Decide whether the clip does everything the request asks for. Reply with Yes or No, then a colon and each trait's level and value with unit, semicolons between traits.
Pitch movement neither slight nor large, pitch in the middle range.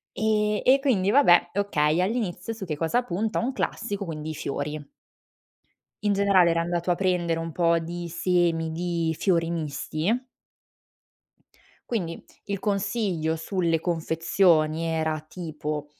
Yes: average, 3.7 semitones; medium, 175 Hz